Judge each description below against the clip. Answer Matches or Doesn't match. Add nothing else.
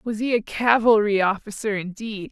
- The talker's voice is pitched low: Doesn't match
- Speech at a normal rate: Matches